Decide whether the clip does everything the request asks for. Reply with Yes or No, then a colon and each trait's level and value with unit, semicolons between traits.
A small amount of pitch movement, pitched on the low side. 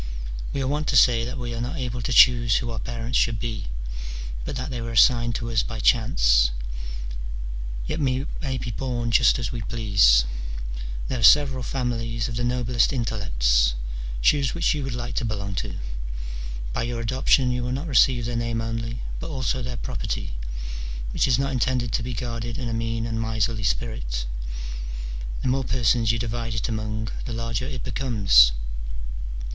Yes: narrow, 2.0 semitones; low, 120 Hz